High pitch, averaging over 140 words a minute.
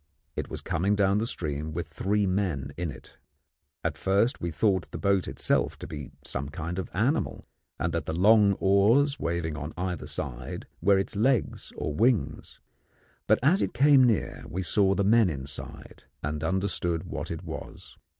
No: very low, 95 Hz; average, 180 wpm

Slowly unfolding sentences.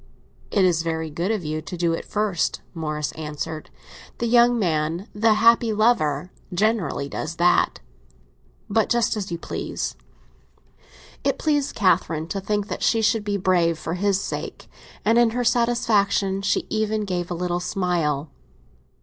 No: average, 150 wpm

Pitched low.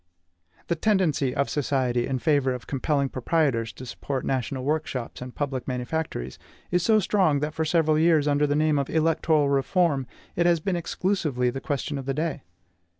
No: medium, 145 Hz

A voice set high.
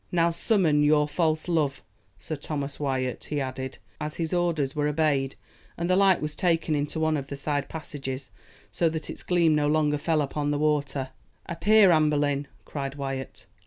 No: medium, 150 Hz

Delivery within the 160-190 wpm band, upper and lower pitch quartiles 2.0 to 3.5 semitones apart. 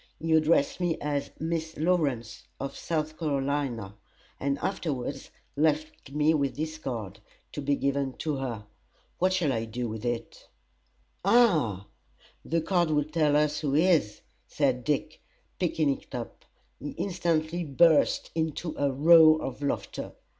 No: average, 140 wpm; average, 3.1 semitones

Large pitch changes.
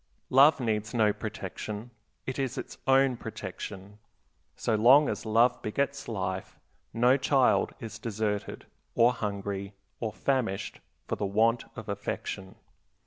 No: average, 3.5 semitones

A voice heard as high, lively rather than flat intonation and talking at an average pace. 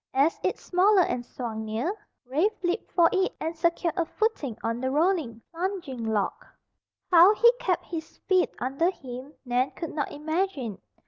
Yes: very high, 320 Hz; wide, 6.4 semitones; average, 165 wpm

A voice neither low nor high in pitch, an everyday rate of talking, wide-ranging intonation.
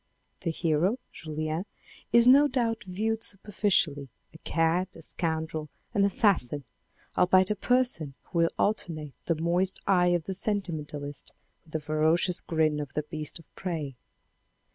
No: medium, 170 Hz; average, 145 wpm; average, 4.1 semitones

